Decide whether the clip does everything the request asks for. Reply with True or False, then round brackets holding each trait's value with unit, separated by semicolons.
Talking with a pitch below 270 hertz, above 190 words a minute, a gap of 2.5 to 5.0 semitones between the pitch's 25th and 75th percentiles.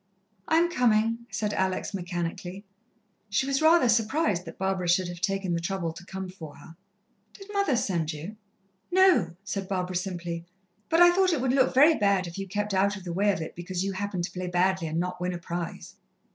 True (190 Hz; 205 wpm; 4.5 semitones)